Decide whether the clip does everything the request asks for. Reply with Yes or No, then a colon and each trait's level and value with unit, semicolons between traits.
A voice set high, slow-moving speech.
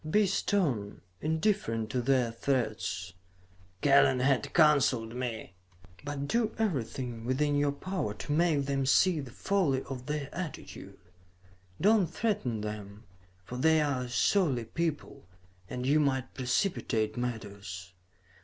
No: low, 135 Hz; slow, 130 wpm